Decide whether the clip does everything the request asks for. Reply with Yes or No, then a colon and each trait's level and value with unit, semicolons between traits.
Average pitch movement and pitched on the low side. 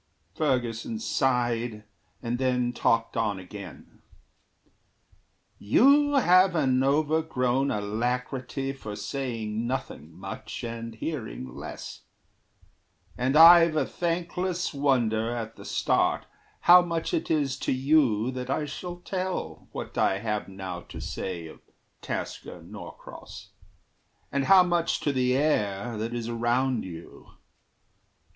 No: wide, 5.7 semitones; low, 125 Hz